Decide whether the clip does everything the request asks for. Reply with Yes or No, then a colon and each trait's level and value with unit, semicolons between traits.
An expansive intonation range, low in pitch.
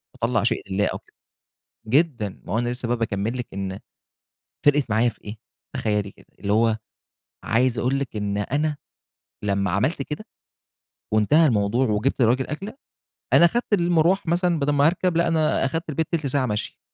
Yes: wide, 6.5 semitones; low, 125 Hz